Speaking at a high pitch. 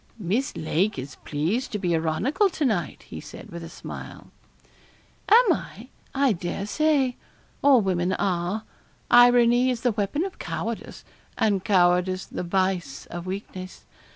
Yes: high, 200 Hz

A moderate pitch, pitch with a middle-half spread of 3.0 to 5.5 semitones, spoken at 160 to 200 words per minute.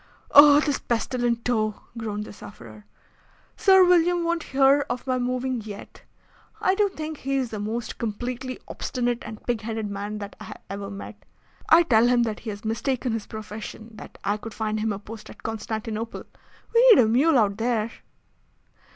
No: high, 230 Hz; average, 3.7 semitones; average, 185 wpm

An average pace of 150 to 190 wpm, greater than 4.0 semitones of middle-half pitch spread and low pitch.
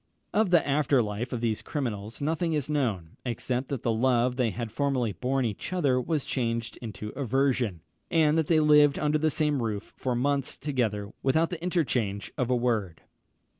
Yes: average, 180 wpm; average, 4.5 semitones; low, 130 Hz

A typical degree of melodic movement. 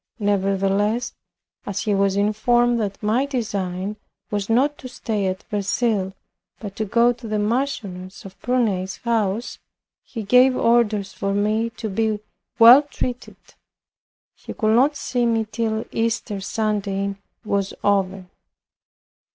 Yes: average, 3.1 semitones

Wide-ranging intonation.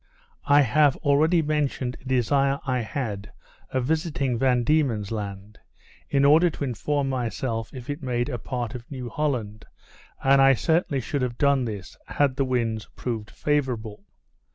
No: average, 3.6 semitones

